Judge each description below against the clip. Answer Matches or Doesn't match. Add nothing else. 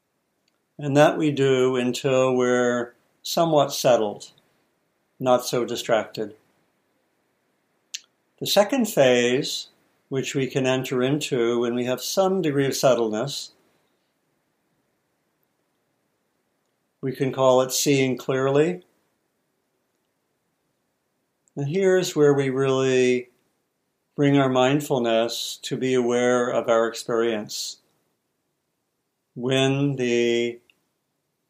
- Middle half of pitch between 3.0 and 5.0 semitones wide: Doesn't match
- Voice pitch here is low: Matches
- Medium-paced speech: Doesn't match